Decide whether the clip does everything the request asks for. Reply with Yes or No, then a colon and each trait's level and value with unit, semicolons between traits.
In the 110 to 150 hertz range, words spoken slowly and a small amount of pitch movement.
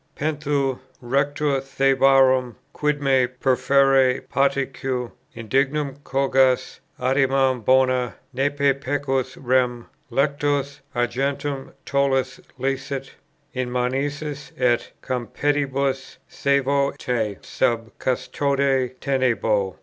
Yes: low, 135 Hz; slow, 80 wpm; narrow, 1.5 semitones